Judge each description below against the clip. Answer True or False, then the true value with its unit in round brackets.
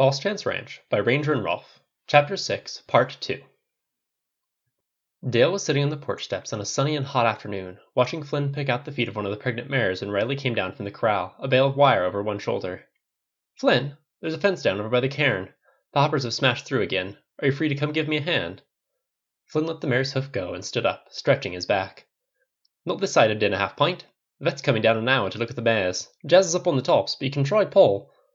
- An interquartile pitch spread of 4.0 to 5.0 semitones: True (4.7 semitones)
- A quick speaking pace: True (245 wpm)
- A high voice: False (140 Hz)